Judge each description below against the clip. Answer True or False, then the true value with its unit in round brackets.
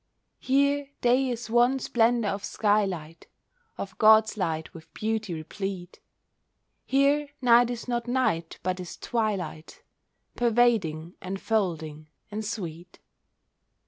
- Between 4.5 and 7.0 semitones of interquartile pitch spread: True (5.3 semitones)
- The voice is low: False (215 Hz)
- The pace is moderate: False (110 wpm)